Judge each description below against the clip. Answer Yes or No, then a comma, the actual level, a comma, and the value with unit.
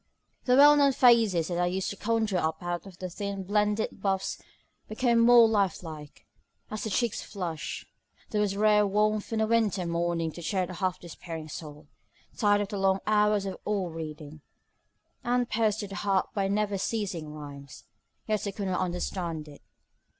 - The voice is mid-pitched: No, high, 195 Hz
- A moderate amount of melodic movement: Yes, average, 3.6 semitones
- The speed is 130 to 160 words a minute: No, average, 190 wpm